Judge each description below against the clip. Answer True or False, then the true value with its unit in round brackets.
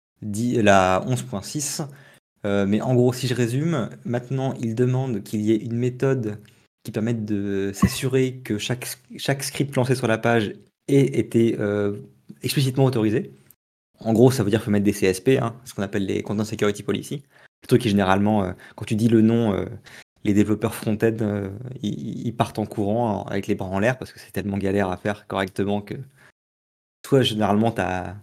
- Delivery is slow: False (190 wpm)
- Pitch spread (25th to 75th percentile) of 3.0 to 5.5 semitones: True (3.4 semitones)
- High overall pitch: False (110 Hz)